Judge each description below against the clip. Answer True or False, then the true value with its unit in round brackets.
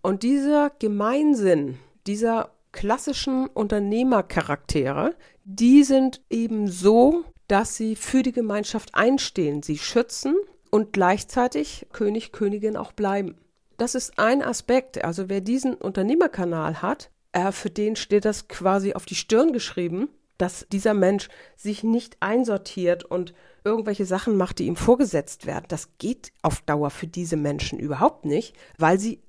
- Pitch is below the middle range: False (210 Hz)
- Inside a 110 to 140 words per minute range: True (135 wpm)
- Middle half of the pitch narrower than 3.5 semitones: False (4.6 semitones)